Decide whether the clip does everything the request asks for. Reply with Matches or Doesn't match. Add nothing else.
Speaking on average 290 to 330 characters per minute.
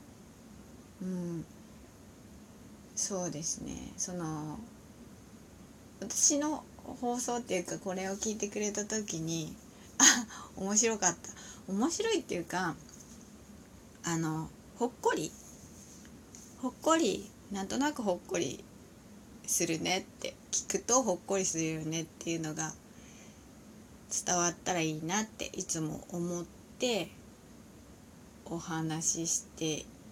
Doesn't match